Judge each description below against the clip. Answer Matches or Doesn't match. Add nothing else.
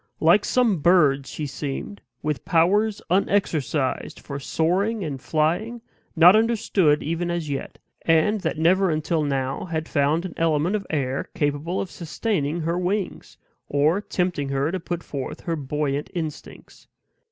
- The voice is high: Doesn't match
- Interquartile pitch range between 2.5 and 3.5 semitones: Doesn't match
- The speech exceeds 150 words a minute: Doesn't match